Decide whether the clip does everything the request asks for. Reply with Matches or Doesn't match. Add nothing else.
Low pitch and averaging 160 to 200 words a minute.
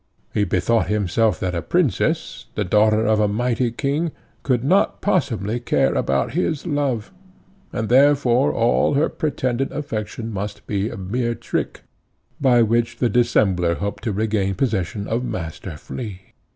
Doesn't match